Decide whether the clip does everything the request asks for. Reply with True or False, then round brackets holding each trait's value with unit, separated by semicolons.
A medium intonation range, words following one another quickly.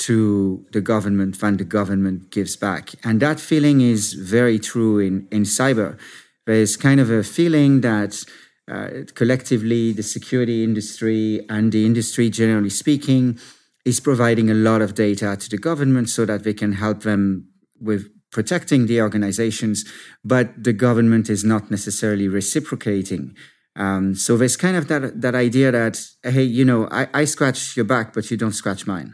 False (3.2 semitones; 165 wpm)